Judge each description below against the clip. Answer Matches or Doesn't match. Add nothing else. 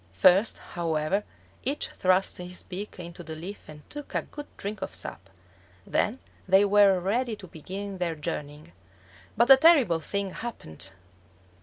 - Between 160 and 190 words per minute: Doesn't match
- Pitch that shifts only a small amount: Doesn't match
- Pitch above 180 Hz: Matches